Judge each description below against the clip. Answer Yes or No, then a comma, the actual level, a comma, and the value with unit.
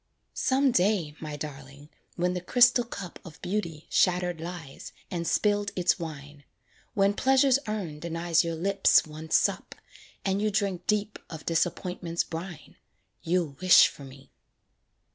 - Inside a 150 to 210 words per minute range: No, average, 140 wpm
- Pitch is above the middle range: No, medium, 175 Hz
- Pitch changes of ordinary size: Yes, average, 3.9 semitones